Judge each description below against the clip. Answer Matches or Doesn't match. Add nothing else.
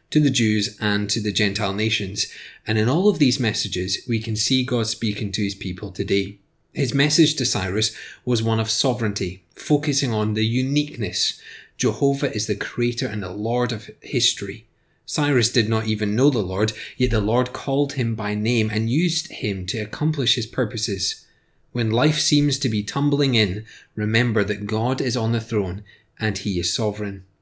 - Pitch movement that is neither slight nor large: Matches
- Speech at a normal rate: Matches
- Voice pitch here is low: Matches